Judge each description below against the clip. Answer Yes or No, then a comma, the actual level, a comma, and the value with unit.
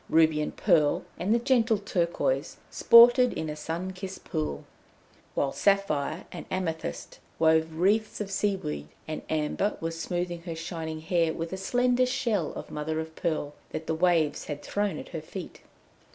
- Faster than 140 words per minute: Yes, average, 165 wpm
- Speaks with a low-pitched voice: No, medium, 170 Hz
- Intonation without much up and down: No, average, 3.9 semitones